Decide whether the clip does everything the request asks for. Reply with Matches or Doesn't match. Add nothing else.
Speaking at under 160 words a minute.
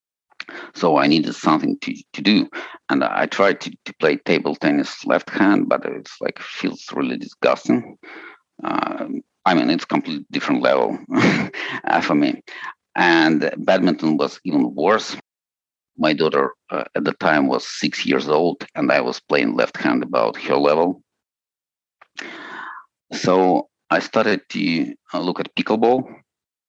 Matches